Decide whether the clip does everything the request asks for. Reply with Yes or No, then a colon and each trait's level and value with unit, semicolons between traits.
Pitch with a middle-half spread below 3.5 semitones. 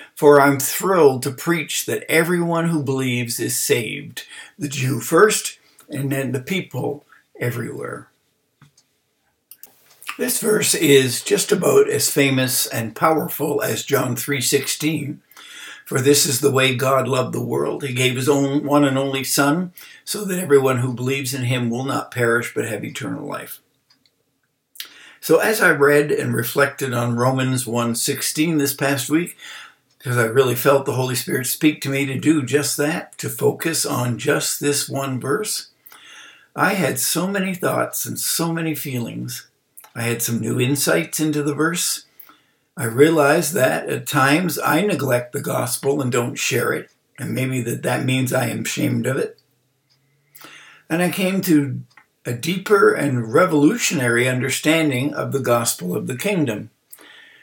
Yes: average, 2.7 semitones